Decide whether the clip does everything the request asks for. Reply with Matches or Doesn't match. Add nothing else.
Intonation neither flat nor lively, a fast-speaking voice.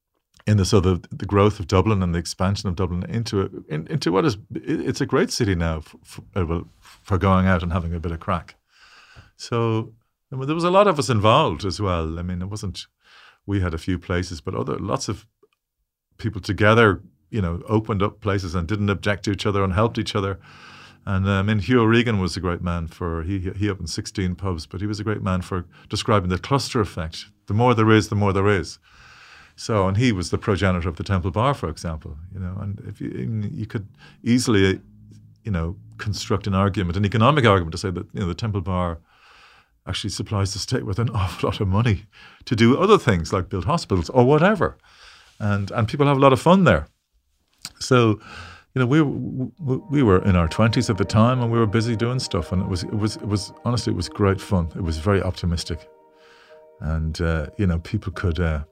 Matches